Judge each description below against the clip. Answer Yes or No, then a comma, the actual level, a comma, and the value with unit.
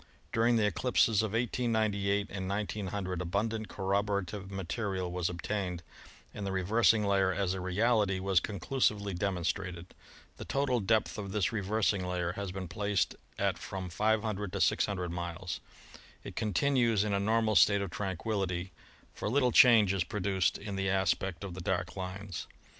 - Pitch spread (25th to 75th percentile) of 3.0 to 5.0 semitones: No, narrow, 2.4 semitones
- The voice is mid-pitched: No, low, 100 Hz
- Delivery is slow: No, average, 155 wpm